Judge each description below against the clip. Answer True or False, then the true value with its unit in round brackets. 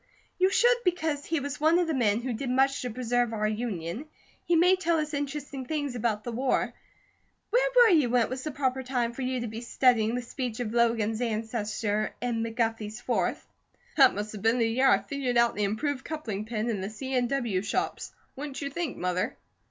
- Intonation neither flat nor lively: True (4.1 semitones)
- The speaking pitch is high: True (245 Hz)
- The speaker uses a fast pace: True (215 wpm)